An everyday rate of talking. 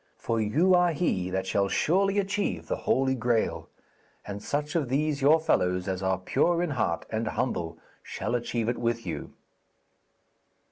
Yes: average, 160 wpm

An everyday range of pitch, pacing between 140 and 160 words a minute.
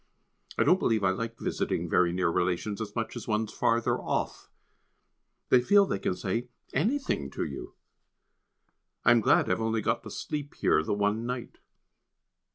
No: average, 4.3 semitones; average, 170 wpm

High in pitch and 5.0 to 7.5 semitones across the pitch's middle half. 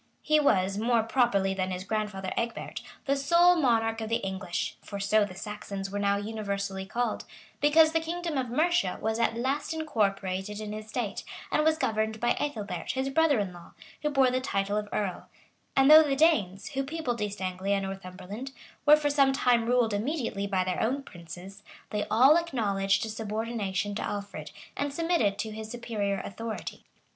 Yes: high, 220 Hz; average, 5.3 semitones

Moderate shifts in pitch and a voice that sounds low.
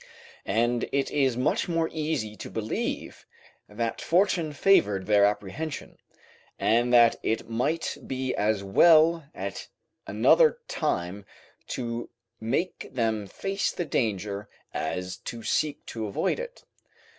No: wide, 6.9 semitones; low, 120 Hz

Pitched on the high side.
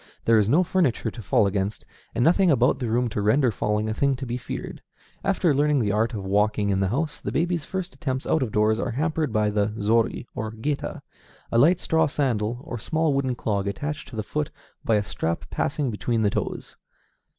No: low, 120 Hz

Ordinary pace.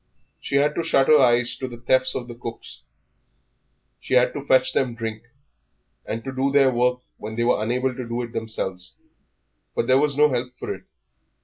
Yes: average, 195 wpm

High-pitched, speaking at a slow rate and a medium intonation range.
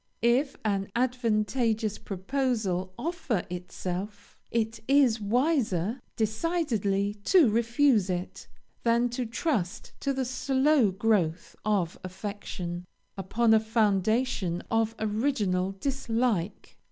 Yes: high, 220 Hz; slow, 100 wpm; average, 4.4 semitones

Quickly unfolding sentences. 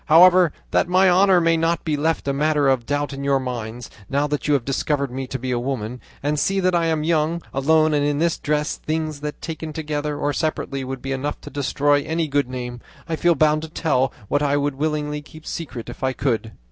Yes: fast, 230 wpm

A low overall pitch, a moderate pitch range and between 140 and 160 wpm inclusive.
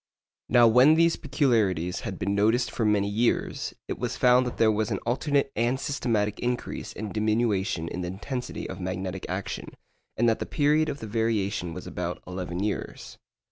No: low, 110 Hz; average, 4.0 semitones; average, 180 wpm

